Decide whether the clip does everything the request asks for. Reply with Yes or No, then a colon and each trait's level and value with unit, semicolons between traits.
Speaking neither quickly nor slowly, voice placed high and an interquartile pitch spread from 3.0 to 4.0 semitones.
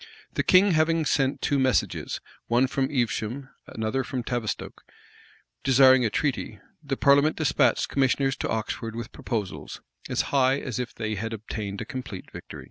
No: average, 155 wpm; low, 130 Hz; average, 3.5 semitones